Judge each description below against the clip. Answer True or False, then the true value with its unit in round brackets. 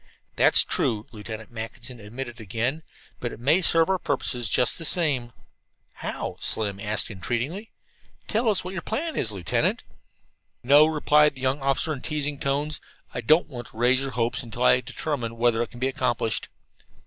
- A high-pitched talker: False (125 Hz)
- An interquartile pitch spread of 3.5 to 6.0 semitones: True (4.6 semitones)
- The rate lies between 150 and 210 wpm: True (170 wpm)